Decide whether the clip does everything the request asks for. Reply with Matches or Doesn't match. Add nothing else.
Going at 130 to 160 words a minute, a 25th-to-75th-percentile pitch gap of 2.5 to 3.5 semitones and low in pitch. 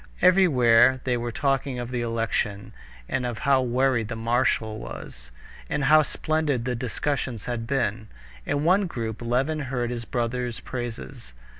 Matches